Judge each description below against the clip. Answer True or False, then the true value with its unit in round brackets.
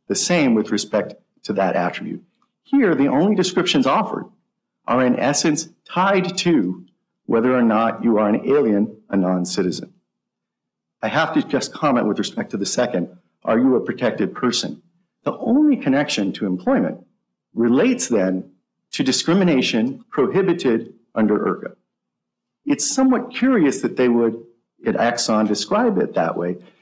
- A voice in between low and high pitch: False (130 Hz)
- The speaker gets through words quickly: False (150 wpm)